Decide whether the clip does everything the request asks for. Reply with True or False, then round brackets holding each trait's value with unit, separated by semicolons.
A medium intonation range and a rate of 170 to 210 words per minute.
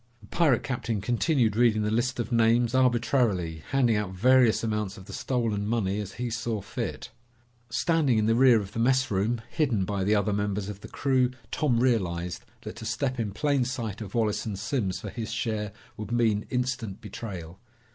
True (3.2 semitones; 185 wpm)